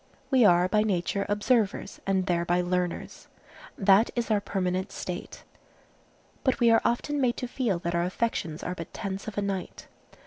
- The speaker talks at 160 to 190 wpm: Yes, average, 170 wpm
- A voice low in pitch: No, high, 195 Hz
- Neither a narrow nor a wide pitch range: Yes, average, 4.1 semitones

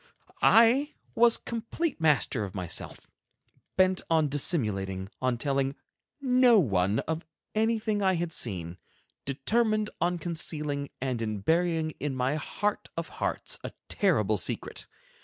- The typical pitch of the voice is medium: Yes, medium, 155 Hz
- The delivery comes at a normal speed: No, slow, 125 wpm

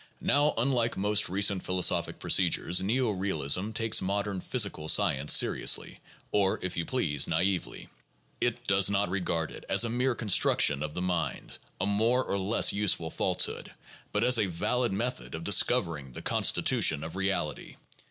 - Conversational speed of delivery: Yes, average, 155 wpm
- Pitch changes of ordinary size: Yes, average, 4.8 semitones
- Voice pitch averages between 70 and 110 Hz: Yes, low, 100 Hz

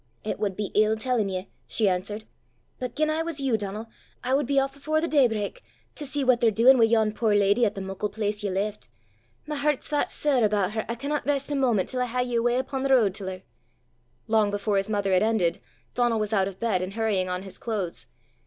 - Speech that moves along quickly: Yes, fast, 240 wpm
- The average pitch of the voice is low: No, high, 220 Hz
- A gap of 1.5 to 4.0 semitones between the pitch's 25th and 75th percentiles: No, average, 4.4 semitones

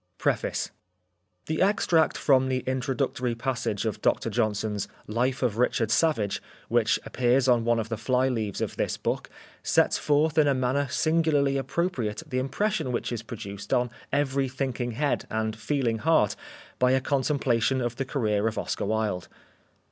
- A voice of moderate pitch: No, low, 125 Hz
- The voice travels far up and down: No, average, 3.6 semitones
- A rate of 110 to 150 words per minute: No, average, 160 wpm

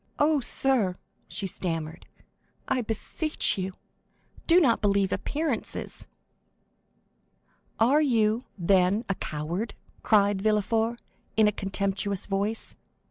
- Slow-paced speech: Yes, slow, 100 wpm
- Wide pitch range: No, average, 3.6 semitones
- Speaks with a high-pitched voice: Yes, high, 210 Hz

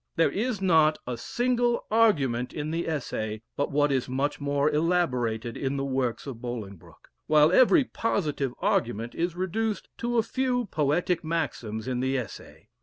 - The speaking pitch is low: No, medium, 150 Hz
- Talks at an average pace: Yes, average, 160 wpm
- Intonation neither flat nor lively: No, wide, 6.8 semitones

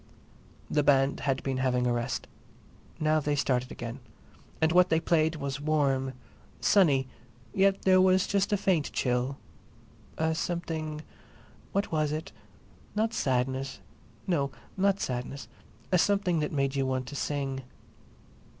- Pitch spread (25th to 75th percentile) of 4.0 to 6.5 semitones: Yes, average, 4.4 semitones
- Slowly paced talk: Yes, slow, 125 wpm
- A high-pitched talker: No, medium, 145 Hz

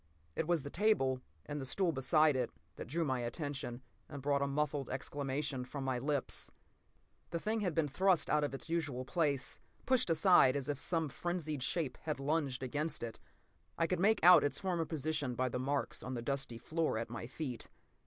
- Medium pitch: Yes, medium, 145 Hz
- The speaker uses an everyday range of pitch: Yes, average, 3.9 semitones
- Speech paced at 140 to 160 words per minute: No, average, 200 wpm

